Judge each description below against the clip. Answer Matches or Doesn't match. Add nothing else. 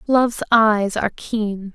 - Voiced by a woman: Matches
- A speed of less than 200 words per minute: Matches